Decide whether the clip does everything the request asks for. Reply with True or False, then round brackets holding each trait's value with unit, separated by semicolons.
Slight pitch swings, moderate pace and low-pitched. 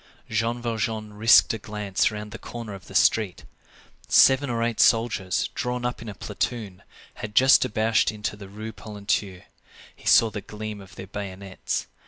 True (2.2 semitones; 170 wpm; 110 Hz)